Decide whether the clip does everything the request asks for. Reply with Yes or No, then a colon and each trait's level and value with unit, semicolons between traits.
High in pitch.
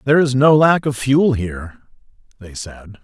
No: low, 125 Hz